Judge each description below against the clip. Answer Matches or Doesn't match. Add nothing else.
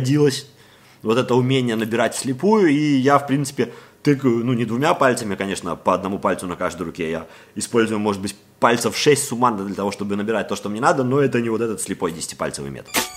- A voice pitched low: Matches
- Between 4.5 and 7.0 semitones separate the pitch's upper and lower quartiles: Matches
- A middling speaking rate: Doesn't match